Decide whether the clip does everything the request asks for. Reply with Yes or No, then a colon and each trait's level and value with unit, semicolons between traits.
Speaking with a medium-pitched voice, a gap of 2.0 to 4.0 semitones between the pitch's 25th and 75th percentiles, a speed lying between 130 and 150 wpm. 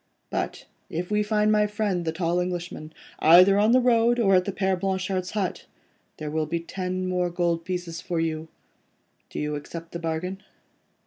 No: medium, 180 Hz; average, 2.9 semitones; average, 180 wpm